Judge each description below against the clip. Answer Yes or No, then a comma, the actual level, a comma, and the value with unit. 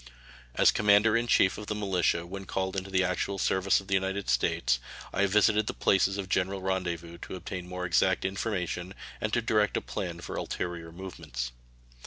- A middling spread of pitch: No, narrow, 1.9 semitones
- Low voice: Yes, very low, 95 Hz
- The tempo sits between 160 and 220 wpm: Yes, average, 190 wpm